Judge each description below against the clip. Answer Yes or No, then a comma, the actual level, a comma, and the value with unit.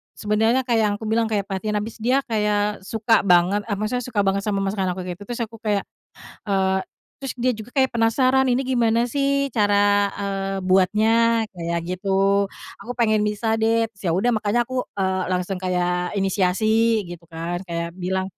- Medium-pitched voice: No, high, 210 Hz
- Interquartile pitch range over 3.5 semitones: No, average, 3.2 semitones